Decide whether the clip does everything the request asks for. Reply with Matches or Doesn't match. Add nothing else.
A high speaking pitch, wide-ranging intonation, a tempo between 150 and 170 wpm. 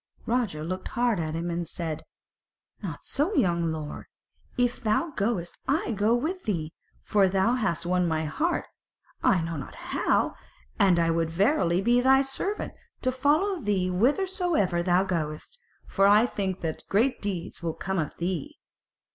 Matches